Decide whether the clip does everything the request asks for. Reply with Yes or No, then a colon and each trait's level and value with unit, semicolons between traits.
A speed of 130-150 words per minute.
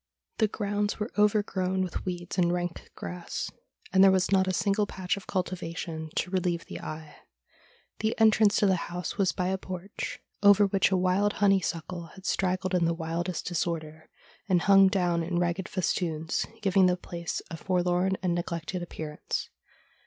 No: average, 165 wpm